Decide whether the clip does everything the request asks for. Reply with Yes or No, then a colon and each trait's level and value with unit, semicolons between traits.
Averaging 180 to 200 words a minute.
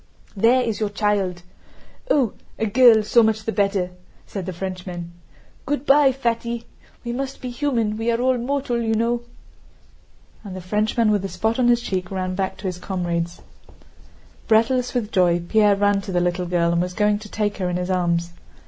Yes: average, 190 wpm